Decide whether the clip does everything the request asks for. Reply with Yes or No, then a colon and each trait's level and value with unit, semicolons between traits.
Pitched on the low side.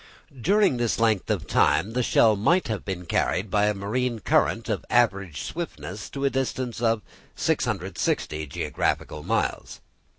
Yes: low, 110 Hz